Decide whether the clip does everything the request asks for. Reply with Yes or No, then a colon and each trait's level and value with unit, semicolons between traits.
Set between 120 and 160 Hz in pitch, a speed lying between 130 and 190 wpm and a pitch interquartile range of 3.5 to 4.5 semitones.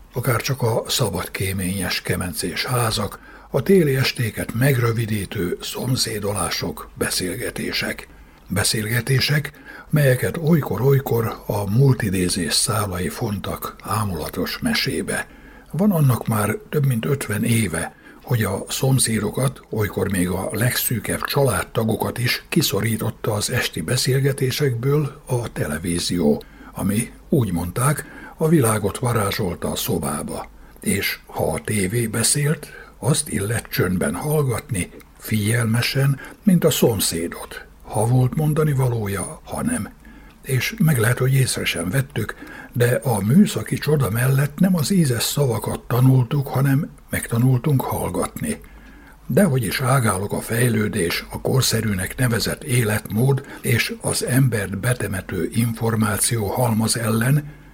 No: low, 125 Hz; average, 110 wpm; average, 4.2 semitones